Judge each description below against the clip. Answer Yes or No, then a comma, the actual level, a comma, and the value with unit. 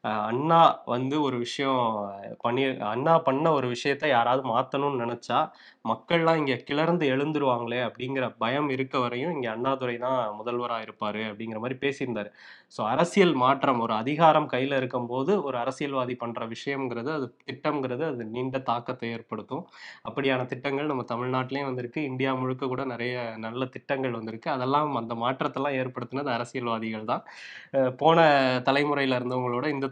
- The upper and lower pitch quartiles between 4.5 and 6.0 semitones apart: No, average, 2.7 semitones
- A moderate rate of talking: No, fast, 135 wpm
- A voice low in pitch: Yes, low, 130 Hz